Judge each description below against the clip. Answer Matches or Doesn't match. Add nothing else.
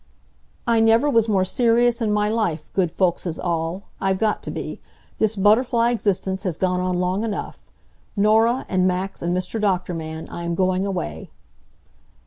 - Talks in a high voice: Matches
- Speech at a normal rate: Matches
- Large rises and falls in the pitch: Doesn't match